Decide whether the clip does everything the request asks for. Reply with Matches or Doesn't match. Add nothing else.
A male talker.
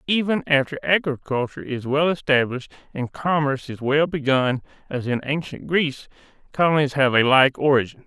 Matches